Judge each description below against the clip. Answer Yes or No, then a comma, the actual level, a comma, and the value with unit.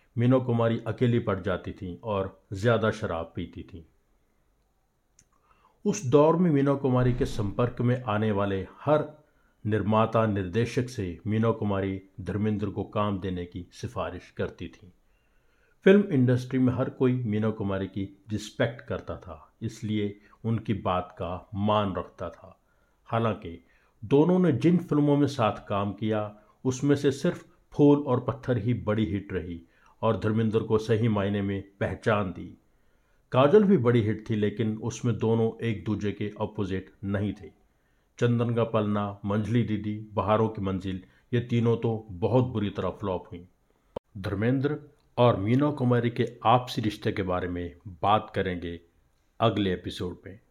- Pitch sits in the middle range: No, low, 110 Hz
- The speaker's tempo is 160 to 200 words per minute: No, average, 150 wpm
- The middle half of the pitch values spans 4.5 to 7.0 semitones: No, average, 3.7 semitones